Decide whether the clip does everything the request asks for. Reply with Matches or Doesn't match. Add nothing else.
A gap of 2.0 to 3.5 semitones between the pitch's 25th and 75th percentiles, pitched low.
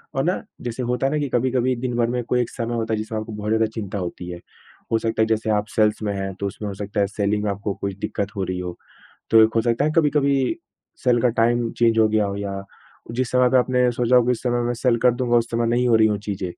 Matches